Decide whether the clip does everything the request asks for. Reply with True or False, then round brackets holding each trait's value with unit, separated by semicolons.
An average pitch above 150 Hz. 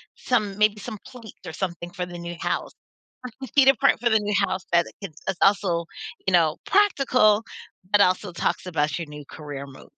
True (190 Hz)